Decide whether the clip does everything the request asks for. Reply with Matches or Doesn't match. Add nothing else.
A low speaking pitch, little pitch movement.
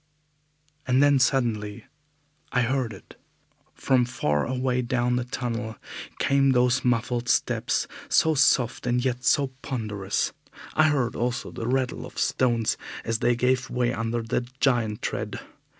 Matches